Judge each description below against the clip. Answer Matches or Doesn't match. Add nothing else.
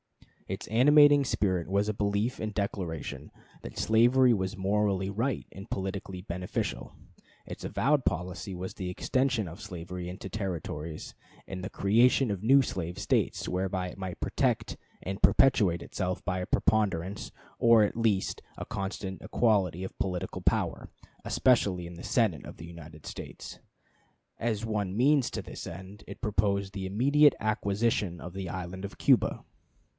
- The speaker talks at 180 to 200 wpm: Doesn't match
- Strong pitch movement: Doesn't match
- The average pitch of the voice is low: Matches